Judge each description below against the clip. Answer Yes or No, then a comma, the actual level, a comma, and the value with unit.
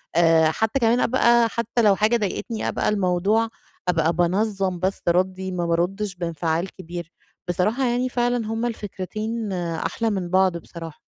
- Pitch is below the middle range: No, high, 190 Hz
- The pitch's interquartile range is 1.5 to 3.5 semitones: No, average, 4.4 semitones